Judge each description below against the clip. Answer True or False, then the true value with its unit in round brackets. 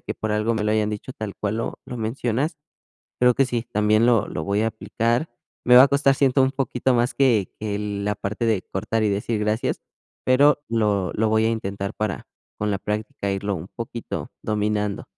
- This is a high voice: False (110 Hz)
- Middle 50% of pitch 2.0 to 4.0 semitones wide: True (2.6 semitones)